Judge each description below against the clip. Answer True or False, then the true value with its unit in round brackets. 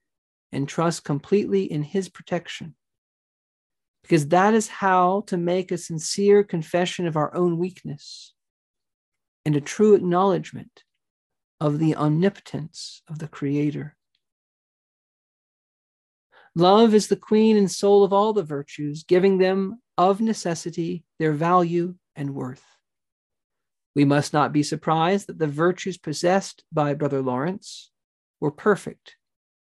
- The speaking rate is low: True (125 wpm)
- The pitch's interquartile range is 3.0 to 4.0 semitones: False (4.4 semitones)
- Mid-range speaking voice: True (175 Hz)